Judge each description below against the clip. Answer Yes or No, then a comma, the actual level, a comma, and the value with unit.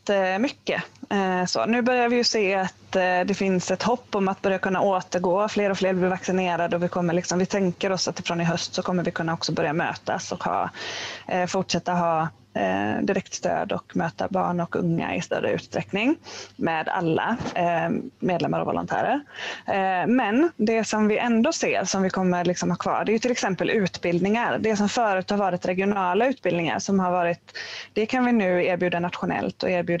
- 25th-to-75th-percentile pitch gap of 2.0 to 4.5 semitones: Yes, average, 3.4 semitones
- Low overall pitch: No, high, 190 Hz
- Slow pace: No, average, 190 wpm